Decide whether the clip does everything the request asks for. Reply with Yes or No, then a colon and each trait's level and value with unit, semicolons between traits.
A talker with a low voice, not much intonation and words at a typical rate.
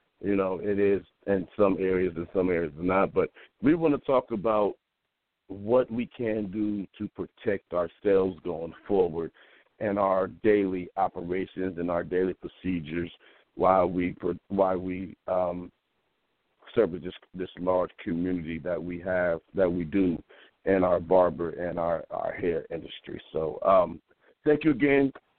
Yes: very low, 95 Hz; narrow, 2.0 semitones; average, 150 wpm